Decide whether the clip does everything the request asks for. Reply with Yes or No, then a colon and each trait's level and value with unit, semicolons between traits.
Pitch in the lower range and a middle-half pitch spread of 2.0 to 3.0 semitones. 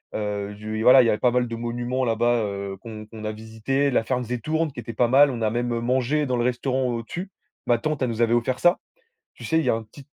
Yes: low, 120 Hz; narrow, 2.6 semitones